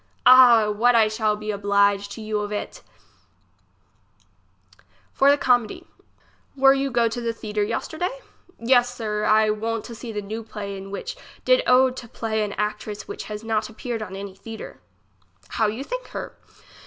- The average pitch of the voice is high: Yes, high, 220 Hz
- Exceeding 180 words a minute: No, average, 170 wpm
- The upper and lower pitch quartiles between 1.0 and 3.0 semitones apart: Yes, narrow, 2.6 semitones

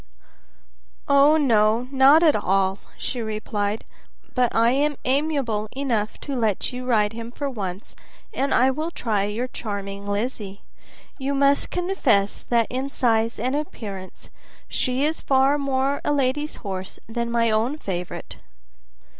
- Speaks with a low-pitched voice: No, high, 240 Hz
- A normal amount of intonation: Yes, average, 4.8 semitones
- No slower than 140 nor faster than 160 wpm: Yes, average, 145 wpm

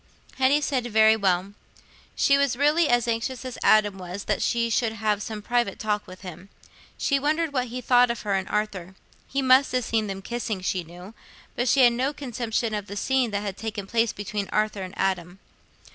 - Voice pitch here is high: Yes, high, 220 Hz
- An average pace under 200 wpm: No, fast, 205 wpm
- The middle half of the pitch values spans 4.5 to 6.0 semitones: No, average, 4.0 semitones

